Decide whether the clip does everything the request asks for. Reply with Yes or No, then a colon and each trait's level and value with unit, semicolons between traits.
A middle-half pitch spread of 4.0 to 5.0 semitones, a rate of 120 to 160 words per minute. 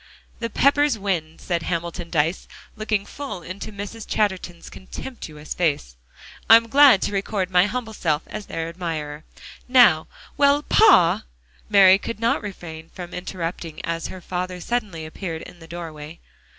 Yes: average, 4.6 semitones; average, 145 wpm